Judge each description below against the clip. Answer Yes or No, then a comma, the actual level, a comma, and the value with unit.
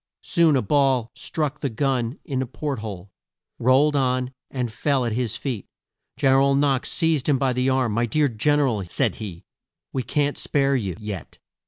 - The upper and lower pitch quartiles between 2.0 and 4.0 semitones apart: Yes, average, 3.5 semitones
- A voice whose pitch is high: No, low, 130 Hz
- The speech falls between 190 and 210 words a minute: Yes, average, 195 wpm